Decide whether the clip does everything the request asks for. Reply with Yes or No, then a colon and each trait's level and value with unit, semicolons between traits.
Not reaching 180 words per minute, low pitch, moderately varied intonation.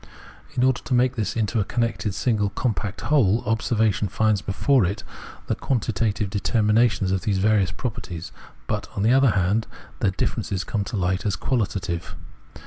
Yes: average, 160 wpm; low, 105 Hz; average, 3.3 semitones